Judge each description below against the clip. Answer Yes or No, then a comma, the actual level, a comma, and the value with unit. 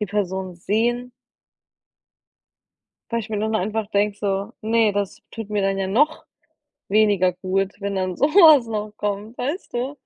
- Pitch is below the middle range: No, high, 210 Hz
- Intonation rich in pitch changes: No, average, 2.9 semitones